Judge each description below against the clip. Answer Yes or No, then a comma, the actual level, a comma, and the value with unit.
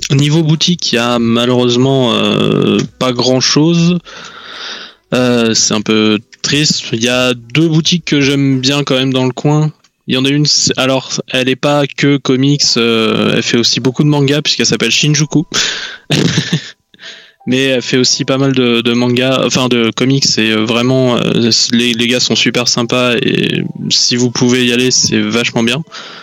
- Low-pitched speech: Yes, low, 130 Hz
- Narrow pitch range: No, average, 3.7 semitones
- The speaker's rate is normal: Yes, average, 180 wpm